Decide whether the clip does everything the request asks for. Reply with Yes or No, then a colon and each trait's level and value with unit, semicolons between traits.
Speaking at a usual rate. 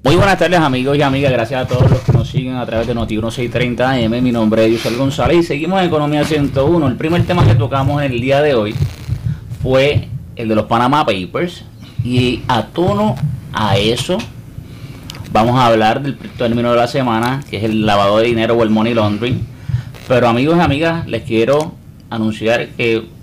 Yes: average, 190 wpm